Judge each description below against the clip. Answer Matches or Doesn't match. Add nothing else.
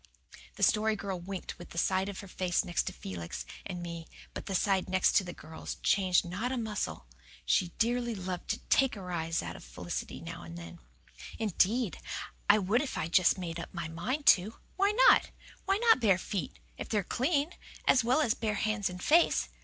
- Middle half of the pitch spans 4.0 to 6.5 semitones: Matches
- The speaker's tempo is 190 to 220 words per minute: Matches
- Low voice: Doesn't match